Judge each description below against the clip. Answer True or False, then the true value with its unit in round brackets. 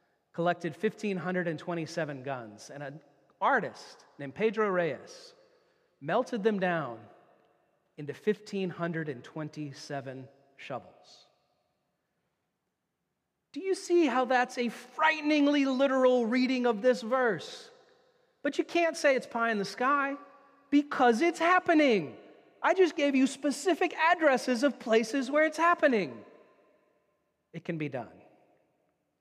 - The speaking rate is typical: False (110 wpm)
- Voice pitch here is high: True (245 Hz)